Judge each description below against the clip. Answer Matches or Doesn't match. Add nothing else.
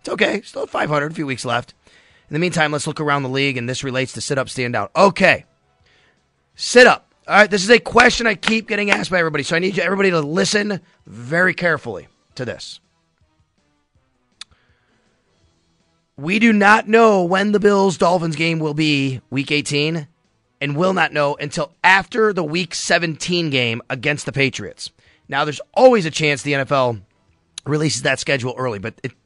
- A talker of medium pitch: Matches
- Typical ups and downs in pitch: Doesn't match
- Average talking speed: Matches